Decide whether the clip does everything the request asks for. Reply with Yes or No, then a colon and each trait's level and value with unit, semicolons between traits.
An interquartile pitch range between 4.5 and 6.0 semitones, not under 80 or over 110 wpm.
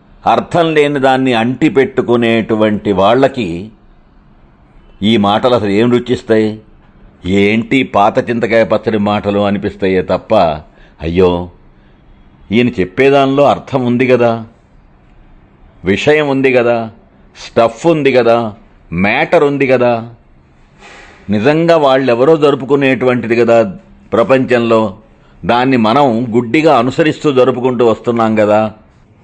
No: average, 3.7 semitones; average, 90 wpm